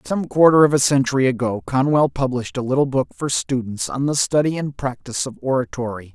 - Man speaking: Yes, male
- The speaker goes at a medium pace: Yes, average, 195 wpm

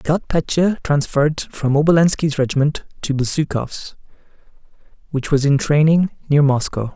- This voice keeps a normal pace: No, slow, 130 wpm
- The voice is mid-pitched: Yes, medium, 145 Hz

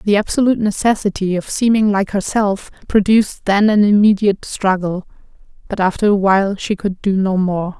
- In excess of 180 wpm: No, average, 160 wpm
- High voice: Yes, high, 200 Hz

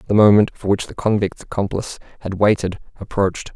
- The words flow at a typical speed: Yes, average, 170 wpm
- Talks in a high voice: No, low, 100 Hz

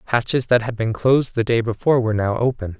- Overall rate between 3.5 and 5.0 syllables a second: No, 6.5 syllables/s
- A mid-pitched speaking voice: No, low, 115 Hz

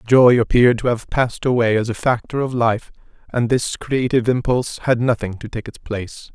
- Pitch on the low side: Yes, low, 120 Hz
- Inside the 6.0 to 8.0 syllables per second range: No, 5.5 syllables/s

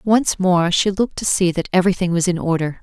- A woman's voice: Yes, female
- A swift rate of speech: Yes, fast, 235 wpm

